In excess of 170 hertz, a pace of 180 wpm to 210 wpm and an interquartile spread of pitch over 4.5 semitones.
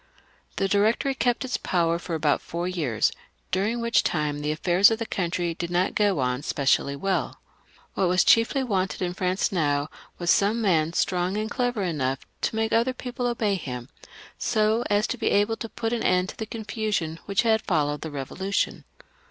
Yes: high, 190 Hz; average, 195 wpm; average, 5.2 semitones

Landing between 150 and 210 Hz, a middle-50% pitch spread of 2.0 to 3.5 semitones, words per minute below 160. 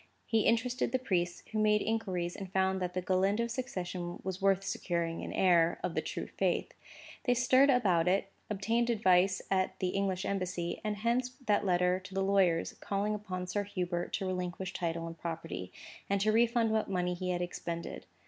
No: high, 190 Hz; average, 3.0 semitones; average, 185 wpm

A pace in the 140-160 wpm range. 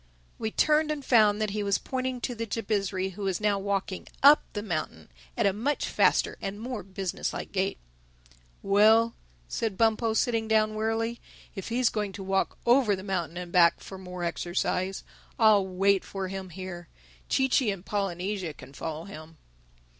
No: average, 175 wpm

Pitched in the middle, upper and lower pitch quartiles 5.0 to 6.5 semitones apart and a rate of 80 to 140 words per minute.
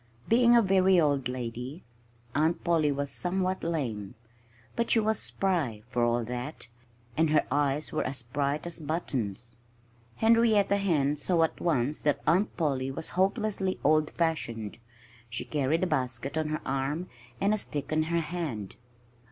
No: medium, 155 Hz; wide, 5.4 semitones; average, 155 wpm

